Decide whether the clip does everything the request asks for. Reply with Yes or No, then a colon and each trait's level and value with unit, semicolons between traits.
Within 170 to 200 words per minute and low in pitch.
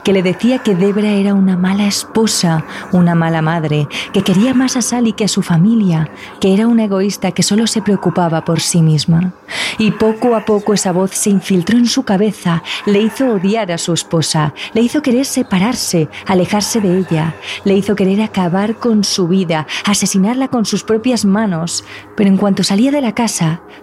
No: fast, 190 wpm; high, 200 Hz